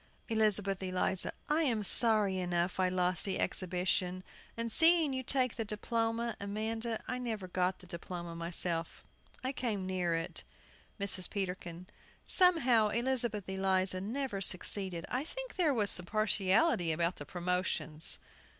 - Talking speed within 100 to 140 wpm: Yes, slow, 135 wpm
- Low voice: No, high, 195 Hz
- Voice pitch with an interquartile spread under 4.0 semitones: No, average, 4.3 semitones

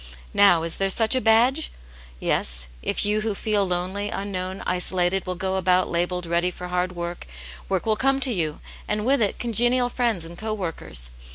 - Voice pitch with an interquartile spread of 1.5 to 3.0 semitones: No, average, 3.7 semitones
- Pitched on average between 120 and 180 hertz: No, high, 190 Hz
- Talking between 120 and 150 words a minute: No, average, 185 wpm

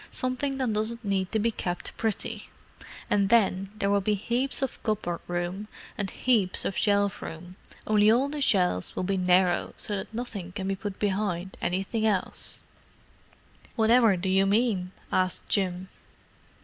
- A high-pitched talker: Yes, high, 200 Hz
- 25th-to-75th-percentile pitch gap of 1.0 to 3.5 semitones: Yes, average, 3.0 semitones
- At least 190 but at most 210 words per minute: No, average, 155 wpm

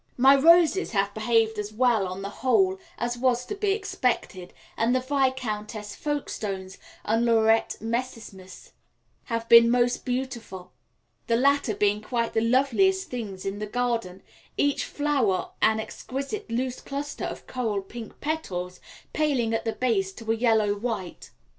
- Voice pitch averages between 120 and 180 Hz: No, high, 230 Hz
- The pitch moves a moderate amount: Yes, average, 3.8 semitones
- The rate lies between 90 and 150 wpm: Yes, average, 145 wpm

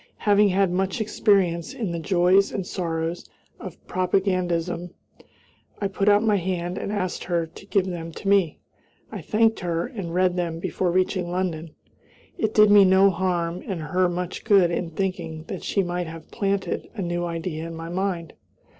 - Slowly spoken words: No, average, 175 wpm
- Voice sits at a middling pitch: Yes, medium, 180 Hz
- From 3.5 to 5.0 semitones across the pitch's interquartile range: No, narrow, 2.5 semitones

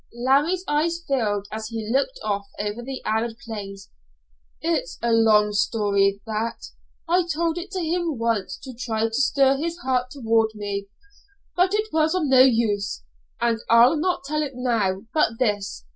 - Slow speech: No, average, 165 wpm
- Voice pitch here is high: Yes, high, 235 Hz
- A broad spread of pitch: Yes, wide, 6.2 semitones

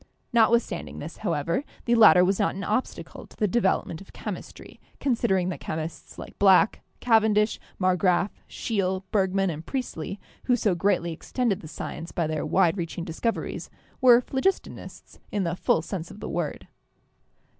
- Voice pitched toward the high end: Yes, high, 195 Hz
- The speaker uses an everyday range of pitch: Yes, average, 4.4 semitones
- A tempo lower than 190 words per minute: Yes, average, 155 wpm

